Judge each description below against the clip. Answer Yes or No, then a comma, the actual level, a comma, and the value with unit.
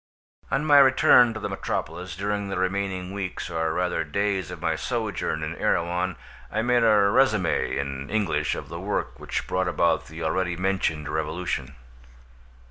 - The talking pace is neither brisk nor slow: Yes, average, 160 wpm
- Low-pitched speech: Yes, very low, 90 Hz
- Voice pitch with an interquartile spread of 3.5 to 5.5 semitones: Yes, average, 3.9 semitones